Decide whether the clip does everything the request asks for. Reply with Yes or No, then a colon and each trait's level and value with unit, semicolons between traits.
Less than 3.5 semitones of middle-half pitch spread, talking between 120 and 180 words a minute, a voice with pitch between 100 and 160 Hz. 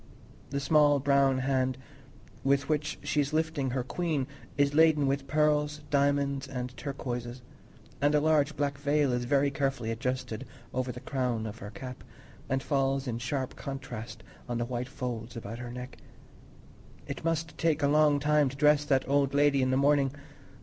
Yes: narrow, 2.5 semitones; average, 170 wpm; medium, 140 Hz